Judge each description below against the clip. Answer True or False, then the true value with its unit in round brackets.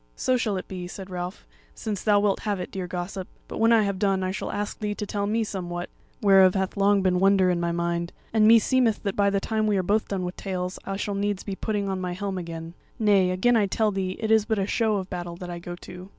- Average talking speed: False (265 wpm)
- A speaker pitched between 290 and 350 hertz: False (195 Hz)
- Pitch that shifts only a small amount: True (2.3 semitones)